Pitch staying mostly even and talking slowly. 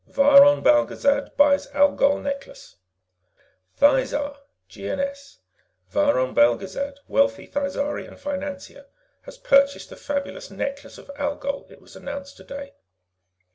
Yes: narrow, 0.5 semitones; slow, 100 wpm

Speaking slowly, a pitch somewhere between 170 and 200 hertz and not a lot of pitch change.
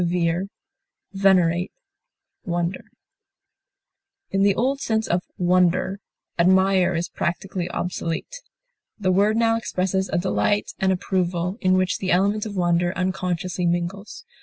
Yes: slow, 120 wpm; medium, 185 Hz; narrow, 2.0 semitones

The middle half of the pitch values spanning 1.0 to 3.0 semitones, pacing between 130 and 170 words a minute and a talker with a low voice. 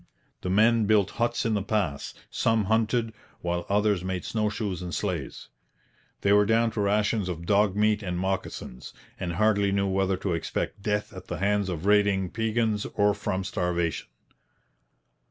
Yes: narrow, 2.5 semitones; average, 165 wpm; low, 100 Hz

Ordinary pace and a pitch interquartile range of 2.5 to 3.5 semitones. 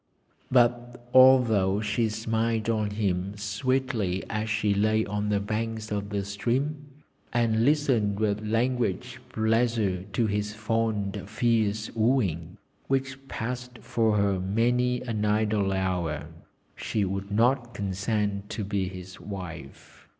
No: slow, 125 wpm; average, 2.8 semitones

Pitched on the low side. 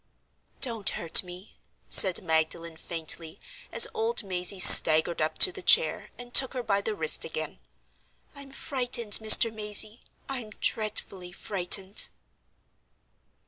No: high, 200 Hz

